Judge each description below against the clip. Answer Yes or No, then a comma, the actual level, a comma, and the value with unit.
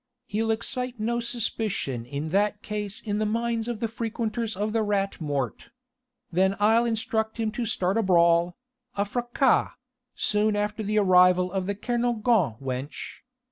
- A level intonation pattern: No, average, 3.5 semitones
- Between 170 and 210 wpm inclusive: No, average, 155 wpm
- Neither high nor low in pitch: No, high, 210 Hz